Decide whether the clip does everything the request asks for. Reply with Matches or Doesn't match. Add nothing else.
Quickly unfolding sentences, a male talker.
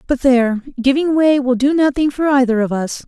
Doesn't match